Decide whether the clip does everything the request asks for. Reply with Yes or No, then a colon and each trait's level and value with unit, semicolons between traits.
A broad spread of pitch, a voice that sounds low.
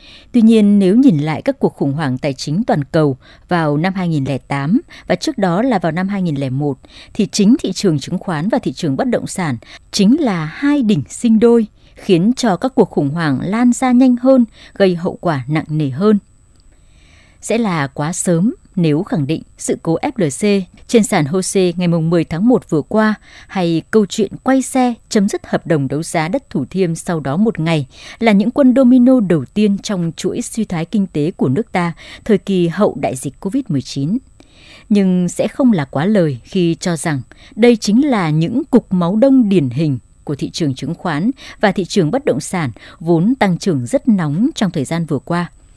No: wide, 6.4 semitones; medium, 185 Hz